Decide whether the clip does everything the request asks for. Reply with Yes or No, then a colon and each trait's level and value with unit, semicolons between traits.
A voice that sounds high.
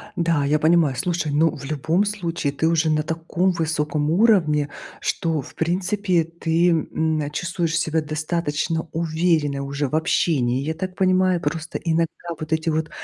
No: medium, 160 Hz